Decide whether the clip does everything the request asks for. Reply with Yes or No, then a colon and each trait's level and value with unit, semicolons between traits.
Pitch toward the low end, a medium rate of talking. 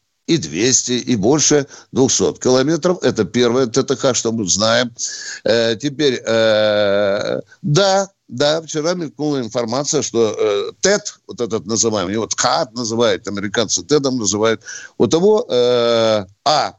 Yes: low, 125 Hz; average, 130 wpm